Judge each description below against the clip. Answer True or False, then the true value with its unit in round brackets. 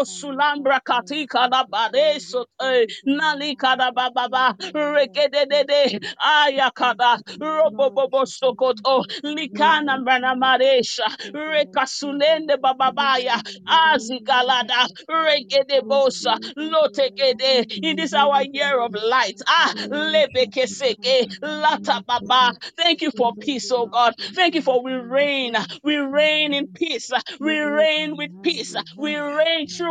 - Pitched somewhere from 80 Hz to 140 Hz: False (275 Hz)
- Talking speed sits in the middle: False (110 wpm)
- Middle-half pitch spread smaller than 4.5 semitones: True (3.0 semitones)